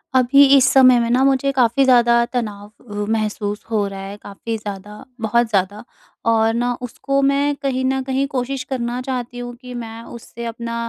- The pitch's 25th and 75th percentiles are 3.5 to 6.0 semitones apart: No, average, 2.8 semitones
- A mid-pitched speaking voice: No, high, 240 Hz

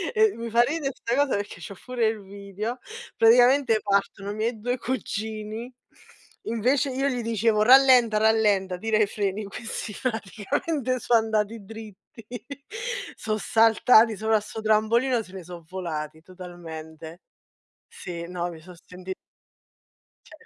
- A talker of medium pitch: No, high, 220 Hz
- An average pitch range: Yes, average, 3.4 semitones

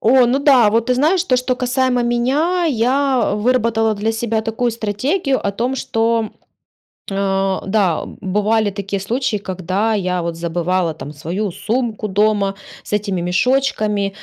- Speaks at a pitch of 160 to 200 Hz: No, high, 220 Hz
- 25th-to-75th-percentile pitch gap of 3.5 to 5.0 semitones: Yes, average, 4.3 semitones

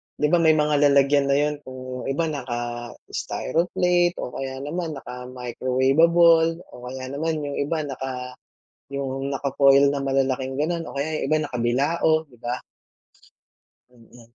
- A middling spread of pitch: Yes, average, 3.1 semitones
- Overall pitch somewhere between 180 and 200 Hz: No, medium, 140 Hz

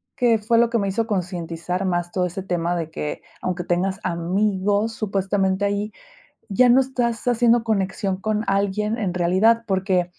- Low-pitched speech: No, high, 195 Hz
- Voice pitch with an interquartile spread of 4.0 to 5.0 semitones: No, average, 3.6 semitones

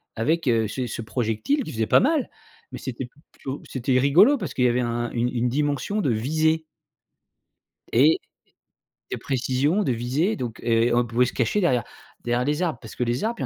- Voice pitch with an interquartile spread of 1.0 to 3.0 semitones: No, average, 4.9 semitones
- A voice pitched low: Yes, low, 130 Hz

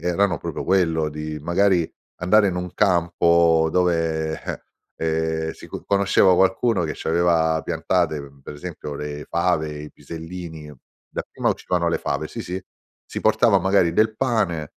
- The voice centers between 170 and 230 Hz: No, very low, 85 Hz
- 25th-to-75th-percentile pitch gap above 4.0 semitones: No, narrow, 2.4 semitones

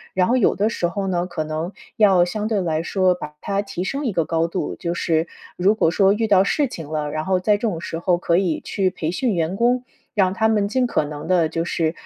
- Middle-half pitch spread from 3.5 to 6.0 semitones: Yes, average, 3.8 semitones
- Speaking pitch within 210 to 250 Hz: No, medium, 185 Hz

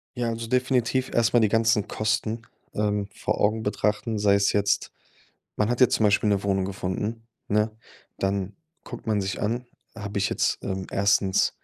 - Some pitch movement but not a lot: No, narrow, 2.2 semitones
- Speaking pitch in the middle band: No, low, 105 Hz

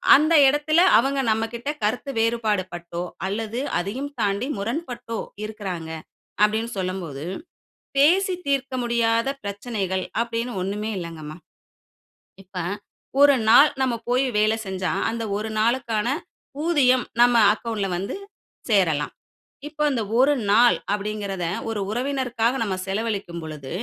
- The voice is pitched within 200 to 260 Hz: Yes, high, 225 Hz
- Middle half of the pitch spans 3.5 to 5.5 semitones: Yes, average, 4.2 semitones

